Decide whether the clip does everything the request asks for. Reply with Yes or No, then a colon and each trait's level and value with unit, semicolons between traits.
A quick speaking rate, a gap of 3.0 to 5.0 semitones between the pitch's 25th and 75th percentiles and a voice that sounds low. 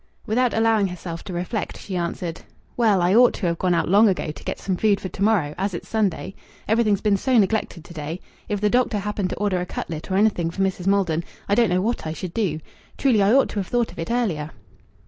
No: fast, 245 wpm; average, 3.8 semitones; high, 195 Hz